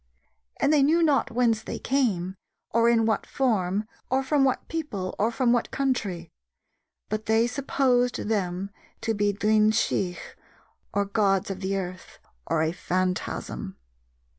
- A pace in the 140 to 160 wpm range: Yes, average, 145 wpm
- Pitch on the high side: Yes, high, 220 Hz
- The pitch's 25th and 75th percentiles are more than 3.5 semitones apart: Yes, average, 4.5 semitones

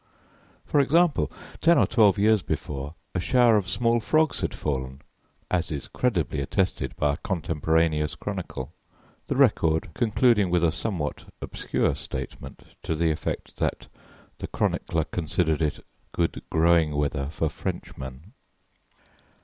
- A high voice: No, very low, 85 Hz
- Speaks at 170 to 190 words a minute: No, slow, 135 wpm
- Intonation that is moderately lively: No, wide, 5.8 semitones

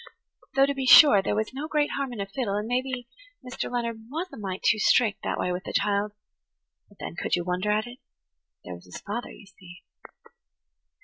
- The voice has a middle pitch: No, high, 215 Hz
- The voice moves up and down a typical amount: Yes, average, 4.6 semitones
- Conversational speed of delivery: No, fast, 225 wpm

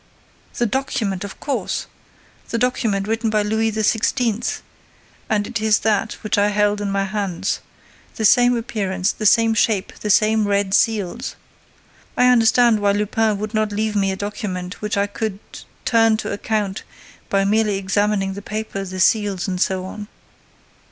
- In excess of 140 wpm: Yes, average, 160 wpm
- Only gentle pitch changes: Yes, narrow, 1.9 semitones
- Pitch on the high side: Yes, high, 210 Hz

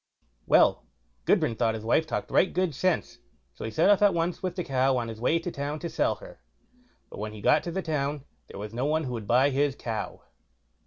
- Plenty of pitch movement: Yes, wide, 6.2 semitones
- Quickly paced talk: Yes, fast, 230 wpm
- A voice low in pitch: No, medium, 145 Hz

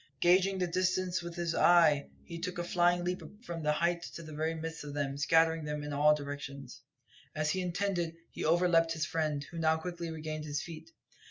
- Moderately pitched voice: Yes, medium, 165 Hz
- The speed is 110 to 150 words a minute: No, average, 200 wpm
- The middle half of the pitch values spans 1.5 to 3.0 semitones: Yes, narrow, 2.5 semitones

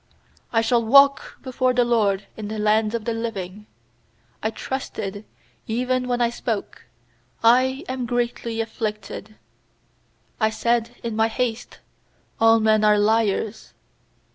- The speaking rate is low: Yes, slow, 130 wpm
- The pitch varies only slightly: Yes, narrow, 2.1 semitones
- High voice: Yes, high, 225 Hz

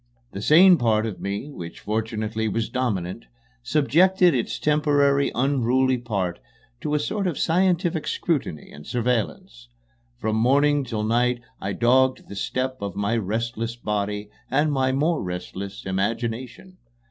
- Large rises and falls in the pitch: No, average, 5.0 semitones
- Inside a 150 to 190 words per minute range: No, slow, 135 wpm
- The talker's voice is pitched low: Yes, low, 120 Hz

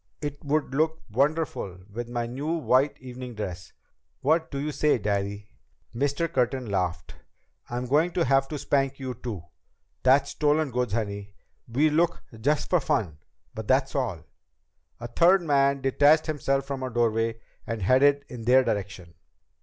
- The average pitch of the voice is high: No, low, 130 Hz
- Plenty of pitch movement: No, average, 4.2 semitones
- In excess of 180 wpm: No, average, 160 wpm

